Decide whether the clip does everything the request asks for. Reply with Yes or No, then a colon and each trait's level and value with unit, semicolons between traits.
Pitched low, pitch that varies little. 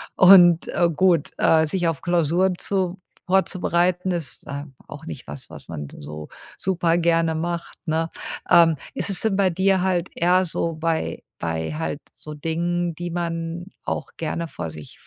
No: medium, 170 Hz; narrow, 2.1 semitones